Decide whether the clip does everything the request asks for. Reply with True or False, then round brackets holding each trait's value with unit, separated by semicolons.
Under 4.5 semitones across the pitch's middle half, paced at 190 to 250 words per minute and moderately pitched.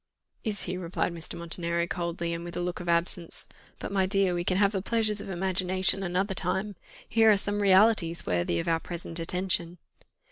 True (2.4 semitones; 200 wpm; 180 Hz)